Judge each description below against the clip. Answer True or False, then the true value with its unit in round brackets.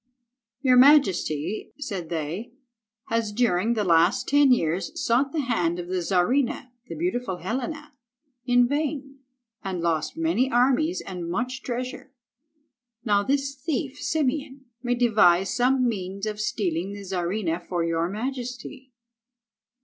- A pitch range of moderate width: False (6.6 semitones)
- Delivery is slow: True (130 wpm)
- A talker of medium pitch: False (235 Hz)